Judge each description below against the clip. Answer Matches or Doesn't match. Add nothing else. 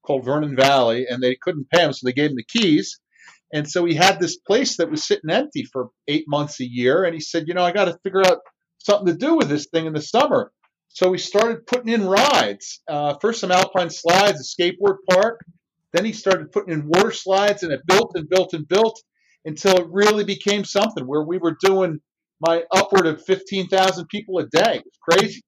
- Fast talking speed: Matches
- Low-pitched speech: Doesn't match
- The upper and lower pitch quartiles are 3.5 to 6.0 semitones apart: Matches